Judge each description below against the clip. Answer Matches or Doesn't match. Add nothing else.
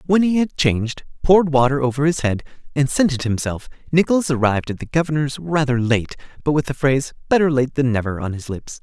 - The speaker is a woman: Doesn't match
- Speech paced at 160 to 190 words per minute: Doesn't match